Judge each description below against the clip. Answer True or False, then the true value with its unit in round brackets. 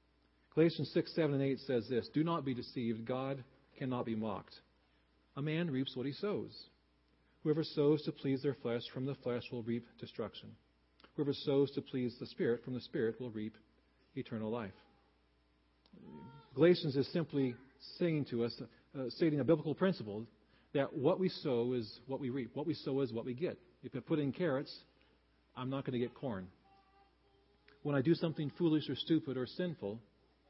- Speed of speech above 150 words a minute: True (180 wpm)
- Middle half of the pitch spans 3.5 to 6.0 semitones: True (4.4 semitones)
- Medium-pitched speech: False (130 Hz)